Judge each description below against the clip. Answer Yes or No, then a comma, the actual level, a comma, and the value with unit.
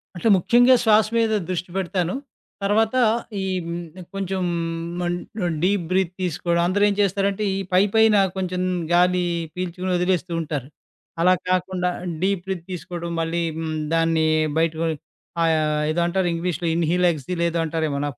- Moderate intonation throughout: No, narrow, 2.2 semitones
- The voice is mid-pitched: Yes, medium, 180 Hz